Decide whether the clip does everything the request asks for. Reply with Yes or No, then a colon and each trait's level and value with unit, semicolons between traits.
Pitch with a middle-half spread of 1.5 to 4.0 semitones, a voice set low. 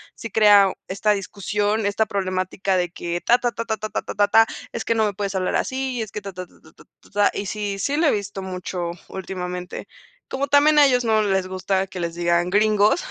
No: average, 2.9 semitones; high, 200 Hz